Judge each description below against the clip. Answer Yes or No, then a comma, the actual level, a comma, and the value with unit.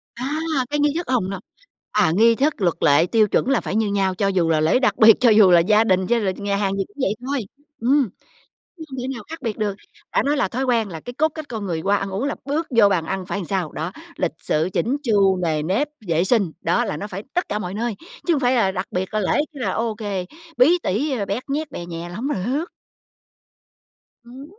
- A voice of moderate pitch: No, high, 210 Hz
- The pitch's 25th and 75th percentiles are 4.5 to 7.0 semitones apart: Yes, average, 5.3 semitones